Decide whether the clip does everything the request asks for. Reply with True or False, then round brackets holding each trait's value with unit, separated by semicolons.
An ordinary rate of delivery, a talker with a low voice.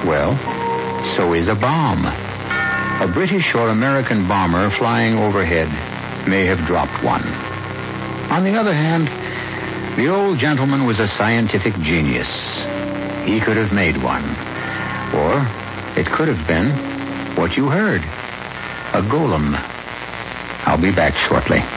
False (125 wpm; 95 Hz)